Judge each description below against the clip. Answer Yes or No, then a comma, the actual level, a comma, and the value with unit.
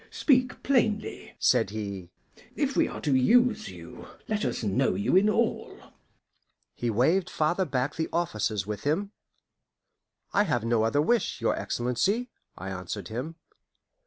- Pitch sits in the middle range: Yes, medium, 145 Hz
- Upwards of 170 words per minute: No, average, 145 wpm